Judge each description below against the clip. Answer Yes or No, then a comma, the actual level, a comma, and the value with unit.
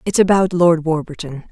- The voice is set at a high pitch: No, medium, 170 Hz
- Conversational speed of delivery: Yes, average, 160 wpm